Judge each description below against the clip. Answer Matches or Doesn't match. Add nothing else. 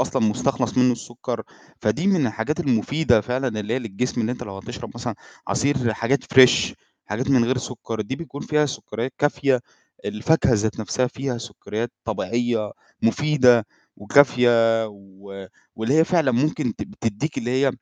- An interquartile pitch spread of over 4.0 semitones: Doesn't match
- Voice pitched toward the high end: Doesn't match